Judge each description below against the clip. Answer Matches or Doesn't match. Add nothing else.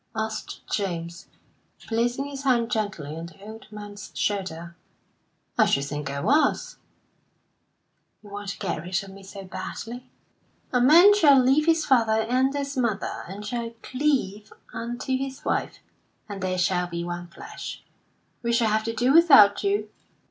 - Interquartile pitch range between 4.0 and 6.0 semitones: Matches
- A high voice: Matches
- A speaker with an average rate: Matches